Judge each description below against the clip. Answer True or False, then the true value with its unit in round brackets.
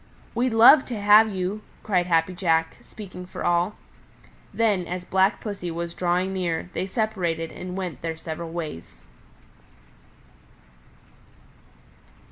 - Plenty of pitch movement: False (3.2 semitones)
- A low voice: False (180 Hz)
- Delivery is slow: True (120 wpm)